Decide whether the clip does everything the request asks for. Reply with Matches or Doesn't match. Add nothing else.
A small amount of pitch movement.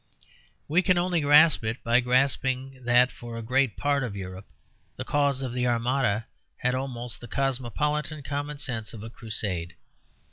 Doesn't match